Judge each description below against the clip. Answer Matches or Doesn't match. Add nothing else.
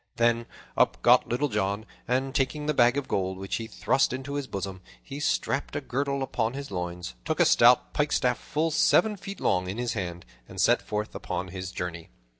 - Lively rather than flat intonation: Matches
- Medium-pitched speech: Doesn't match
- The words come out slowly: Doesn't match